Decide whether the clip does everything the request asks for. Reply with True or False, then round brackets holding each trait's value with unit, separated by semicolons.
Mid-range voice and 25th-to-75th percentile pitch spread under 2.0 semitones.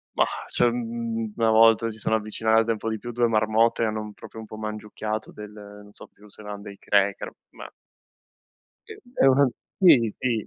False (110 Hz; 1.4 semitones)